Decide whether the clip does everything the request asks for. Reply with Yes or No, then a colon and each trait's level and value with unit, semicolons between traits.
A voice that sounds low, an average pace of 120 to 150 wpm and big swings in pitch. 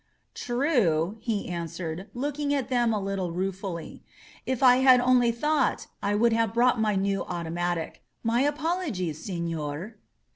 No: high, 215 Hz; average, 145 wpm; wide, 6.2 semitones